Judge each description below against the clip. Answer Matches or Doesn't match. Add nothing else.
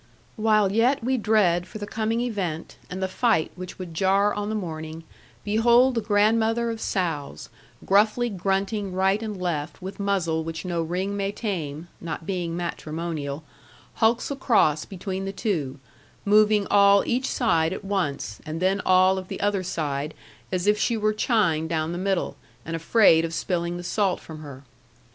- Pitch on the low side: Doesn't match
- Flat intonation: Doesn't match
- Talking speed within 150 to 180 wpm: Matches